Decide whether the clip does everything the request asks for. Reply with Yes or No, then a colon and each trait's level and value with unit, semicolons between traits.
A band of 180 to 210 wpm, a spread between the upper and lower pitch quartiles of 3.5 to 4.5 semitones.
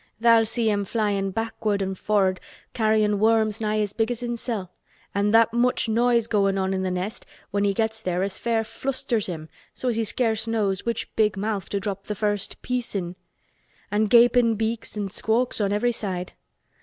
No: average, 190 wpm; narrow, 2.4 semitones